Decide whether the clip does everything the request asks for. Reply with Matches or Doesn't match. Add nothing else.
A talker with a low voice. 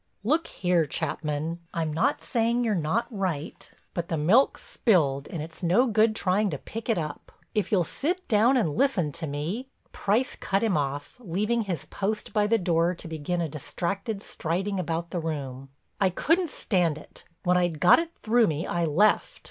Doesn't match